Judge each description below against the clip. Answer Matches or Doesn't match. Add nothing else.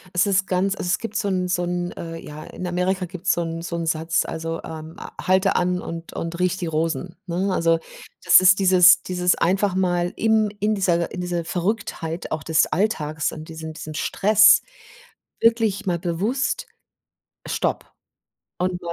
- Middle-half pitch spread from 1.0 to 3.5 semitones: Matches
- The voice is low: Doesn't match